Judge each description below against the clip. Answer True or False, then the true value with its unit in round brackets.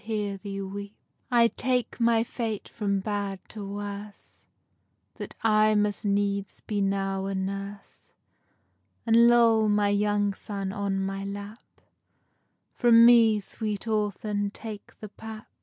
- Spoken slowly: True (125 wpm)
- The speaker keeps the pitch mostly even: True (1.8 semitones)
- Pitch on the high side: True (205 Hz)